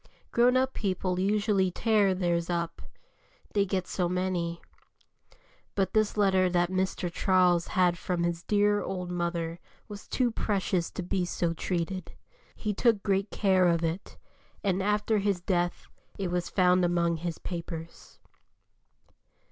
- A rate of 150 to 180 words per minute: No, average, 140 wpm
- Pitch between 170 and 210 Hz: Yes, medium, 185 Hz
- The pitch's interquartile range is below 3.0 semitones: Yes, narrow, 2.4 semitones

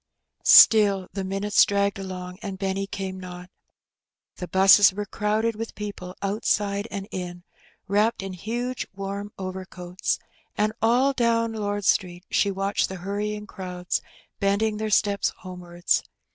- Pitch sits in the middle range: No, high, 200 Hz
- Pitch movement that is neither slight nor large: No, narrow, 1.9 semitones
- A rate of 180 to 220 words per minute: No, slow, 135 wpm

